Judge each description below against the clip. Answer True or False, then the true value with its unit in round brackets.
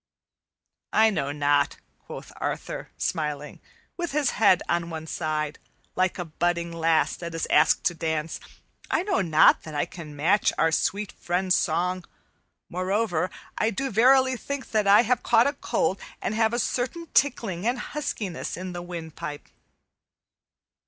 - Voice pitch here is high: False (180 Hz)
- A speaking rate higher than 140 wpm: True (150 wpm)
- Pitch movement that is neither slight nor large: False (5.7 semitones)